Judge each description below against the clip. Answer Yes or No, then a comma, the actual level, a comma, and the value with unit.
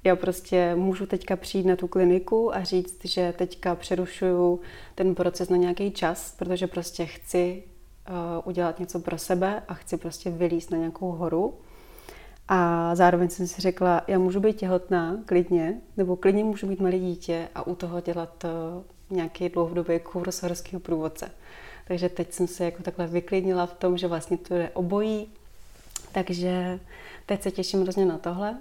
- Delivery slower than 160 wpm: No, fast, 170 wpm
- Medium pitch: Yes, medium, 180 Hz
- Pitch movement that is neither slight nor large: No, narrow, 1.3 semitones